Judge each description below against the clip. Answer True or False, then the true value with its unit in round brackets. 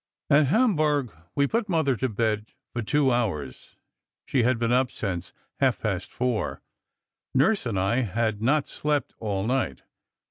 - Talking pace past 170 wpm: False (150 wpm)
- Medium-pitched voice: False (125 Hz)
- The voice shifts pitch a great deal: False (4.8 semitones)